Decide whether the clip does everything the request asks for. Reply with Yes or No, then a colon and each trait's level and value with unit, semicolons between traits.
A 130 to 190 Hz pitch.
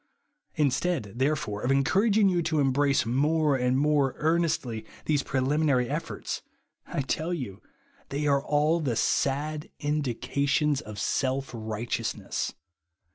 Yes: medium, 140 Hz